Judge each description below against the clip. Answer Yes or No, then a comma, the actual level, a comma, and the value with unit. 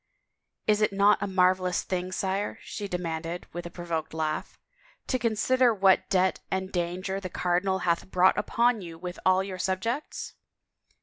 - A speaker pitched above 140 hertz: Yes, medium, 185 Hz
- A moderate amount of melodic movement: No, narrow, 2.1 semitones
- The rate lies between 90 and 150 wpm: No, average, 170 wpm